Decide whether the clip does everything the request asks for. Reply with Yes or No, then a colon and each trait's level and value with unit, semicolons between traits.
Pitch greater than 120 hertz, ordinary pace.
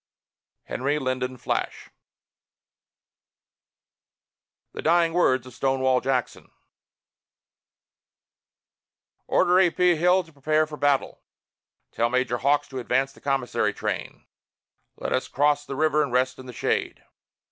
No: low, 135 Hz; slow, 120 wpm